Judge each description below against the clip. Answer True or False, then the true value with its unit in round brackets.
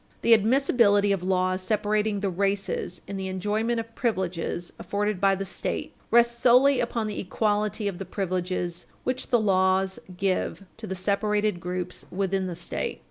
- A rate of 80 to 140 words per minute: False (160 wpm)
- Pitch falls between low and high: False (200 Hz)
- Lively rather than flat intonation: False (2.6 semitones)